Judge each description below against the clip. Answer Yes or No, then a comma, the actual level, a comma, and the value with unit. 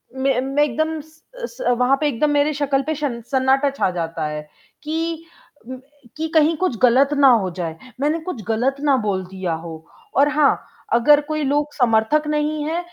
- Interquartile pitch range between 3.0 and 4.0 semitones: No, average, 4.5 semitones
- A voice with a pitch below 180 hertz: No, very high, 280 Hz